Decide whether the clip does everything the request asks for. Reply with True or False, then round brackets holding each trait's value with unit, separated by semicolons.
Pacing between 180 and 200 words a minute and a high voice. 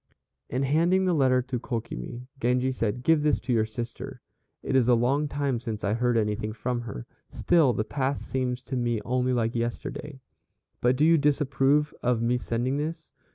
False (185 wpm; 125 Hz)